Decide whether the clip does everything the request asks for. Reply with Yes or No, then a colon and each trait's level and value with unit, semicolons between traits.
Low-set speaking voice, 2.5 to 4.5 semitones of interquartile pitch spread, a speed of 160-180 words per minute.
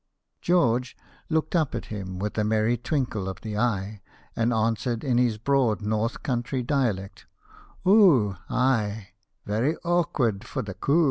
No: low, 115 Hz; average, 4.1 semitones; average, 150 wpm